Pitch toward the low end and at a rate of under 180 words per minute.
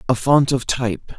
No: low, 125 Hz; fast, 205 wpm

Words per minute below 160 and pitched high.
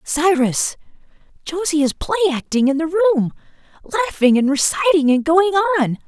Yes: average, 140 wpm; very high, 320 Hz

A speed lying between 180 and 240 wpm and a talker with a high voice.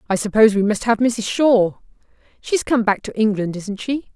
Yes: average, 200 wpm; high, 220 Hz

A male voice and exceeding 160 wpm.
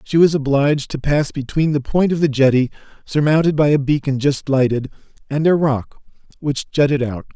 Yes: male; average, 190 wpm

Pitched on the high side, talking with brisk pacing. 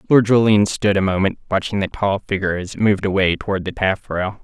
No: low, 100 Hz; fast, 215 wpm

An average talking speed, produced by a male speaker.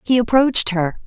No: average, 170 wpm; female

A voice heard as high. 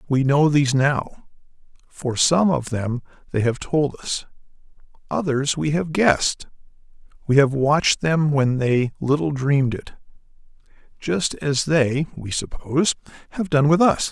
No: medium, 140 Hz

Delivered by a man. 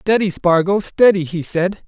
Yes: male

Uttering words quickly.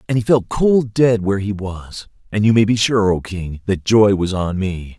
Yes: fast, 240 wpm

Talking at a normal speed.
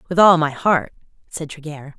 Yes: average, 180 wpm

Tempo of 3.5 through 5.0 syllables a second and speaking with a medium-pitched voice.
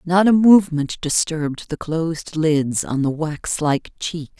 Yes: 4.1 syllables/s; medium, 160 Hz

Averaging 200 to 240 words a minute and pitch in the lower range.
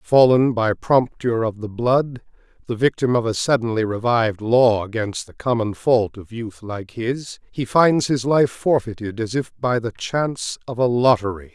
No: average, 175 wpm; low, 115 Hz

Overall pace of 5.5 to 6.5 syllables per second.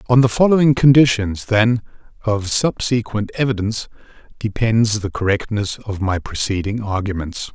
No: 4.9 syllables/s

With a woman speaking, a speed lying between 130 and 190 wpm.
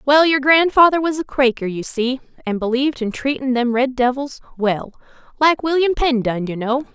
Yes: female; average, 180 wpm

